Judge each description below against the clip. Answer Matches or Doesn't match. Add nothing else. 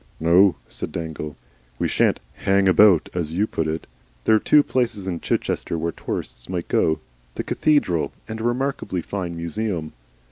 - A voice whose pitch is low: Matches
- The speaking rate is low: Doesn't match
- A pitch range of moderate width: Matches